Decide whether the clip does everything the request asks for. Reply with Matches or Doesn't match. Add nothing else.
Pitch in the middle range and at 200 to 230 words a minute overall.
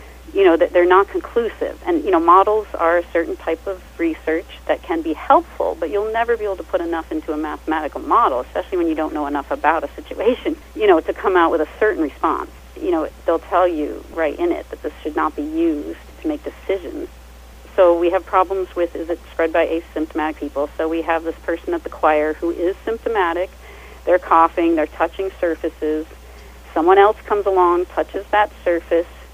Matches